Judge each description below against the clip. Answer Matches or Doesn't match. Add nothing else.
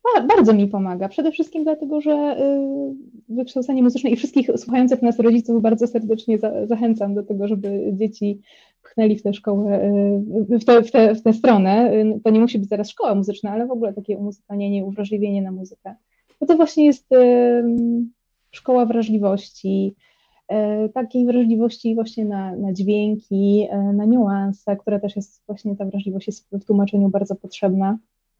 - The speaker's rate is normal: Doesn't match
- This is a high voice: Matches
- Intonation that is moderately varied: Matches